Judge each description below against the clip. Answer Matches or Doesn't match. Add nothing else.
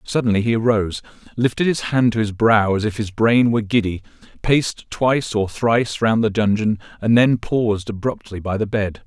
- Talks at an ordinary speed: Matches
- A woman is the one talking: Doesn't match